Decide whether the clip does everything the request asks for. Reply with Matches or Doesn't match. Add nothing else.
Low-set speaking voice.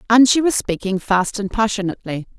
Doesn't match